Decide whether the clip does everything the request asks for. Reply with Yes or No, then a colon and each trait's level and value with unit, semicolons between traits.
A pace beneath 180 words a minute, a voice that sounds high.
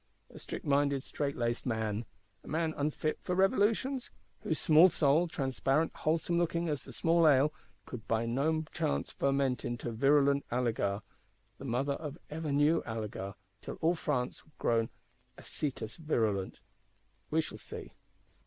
No: average, 140 wpm; medium, 140 Hz